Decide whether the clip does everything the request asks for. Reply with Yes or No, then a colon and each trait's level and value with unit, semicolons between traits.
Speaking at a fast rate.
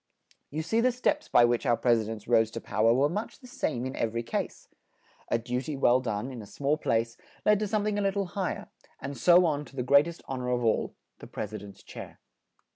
Yes: fast, 270 wpm